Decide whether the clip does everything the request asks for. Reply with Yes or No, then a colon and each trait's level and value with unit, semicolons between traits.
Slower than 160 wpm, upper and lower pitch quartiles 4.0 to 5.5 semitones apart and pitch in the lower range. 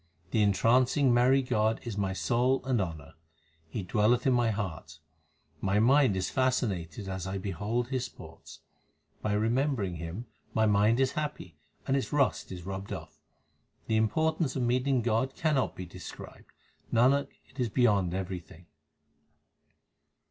Yes: average, 150 wpm; average, 5.2 semitones; low, 110 Hz